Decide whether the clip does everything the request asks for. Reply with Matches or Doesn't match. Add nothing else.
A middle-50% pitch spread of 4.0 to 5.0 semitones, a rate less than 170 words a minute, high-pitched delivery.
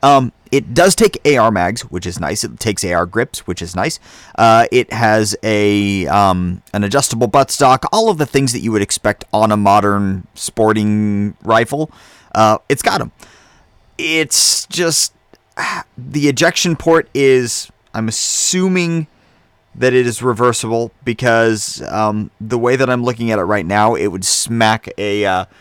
Doesn't match